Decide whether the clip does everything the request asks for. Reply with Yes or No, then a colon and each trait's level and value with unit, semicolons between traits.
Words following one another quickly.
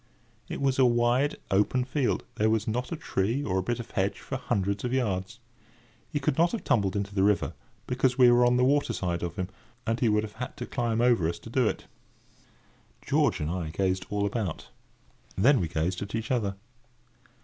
Yes: fast, 210 wpm